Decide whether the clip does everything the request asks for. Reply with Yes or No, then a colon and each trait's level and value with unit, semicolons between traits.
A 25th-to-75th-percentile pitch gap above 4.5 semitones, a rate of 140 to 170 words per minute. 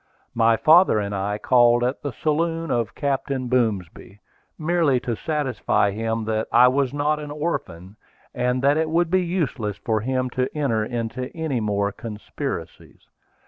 Yes: average, 5.2 semitones; average, 155 wpm